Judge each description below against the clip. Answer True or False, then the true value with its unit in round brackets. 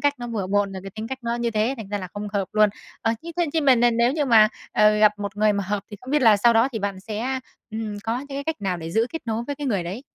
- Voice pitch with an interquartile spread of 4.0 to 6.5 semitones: False (3.5 semitones)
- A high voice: True (220 Hz)